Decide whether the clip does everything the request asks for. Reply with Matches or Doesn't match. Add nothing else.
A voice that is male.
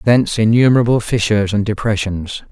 Matches